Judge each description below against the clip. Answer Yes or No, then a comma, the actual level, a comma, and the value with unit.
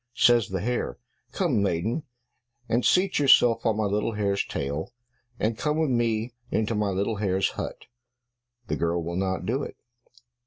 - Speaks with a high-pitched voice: No, low, 110 Hz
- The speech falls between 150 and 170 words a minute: Yes, average, 160 wpm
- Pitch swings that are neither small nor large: Yes, average, 3.8 semitones